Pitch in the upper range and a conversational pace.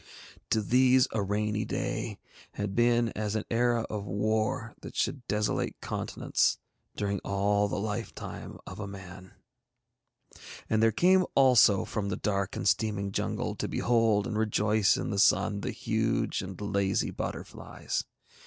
No: low, 105 Hz; average, 150 wpm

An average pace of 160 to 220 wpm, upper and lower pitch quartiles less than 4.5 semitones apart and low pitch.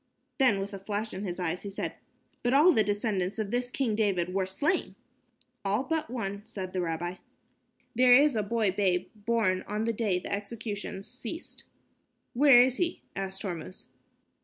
No: average, 175 wpm; average, 4.1 semitones; high, 210 Hz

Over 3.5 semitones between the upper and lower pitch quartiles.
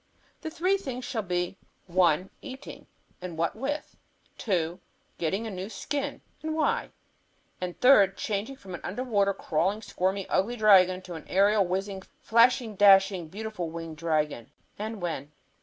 Yes: average, 4.3 semitones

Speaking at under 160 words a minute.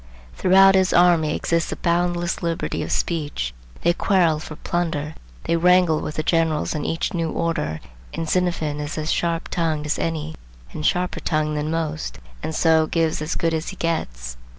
No: average, 175 wpm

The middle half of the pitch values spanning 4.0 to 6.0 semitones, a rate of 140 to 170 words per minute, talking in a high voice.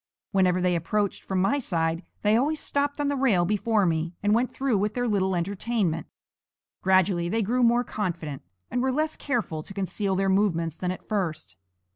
No: average, 5.1 semitones; average, 185 wpm; high, 195 Hz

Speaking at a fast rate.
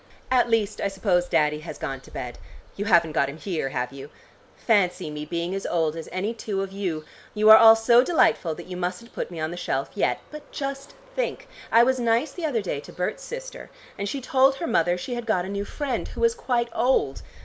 Yes: fast, 230 wpm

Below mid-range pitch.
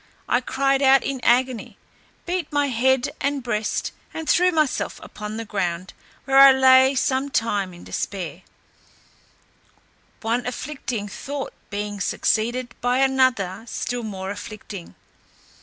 No: high, 245 Hz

